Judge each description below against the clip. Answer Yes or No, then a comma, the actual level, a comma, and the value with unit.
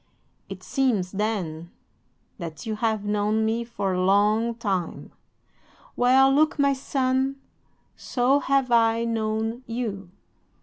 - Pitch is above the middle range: Yes, high, 225 Hz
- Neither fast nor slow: No, slow, 120 wpm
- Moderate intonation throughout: Yes, average, 3.8 semitones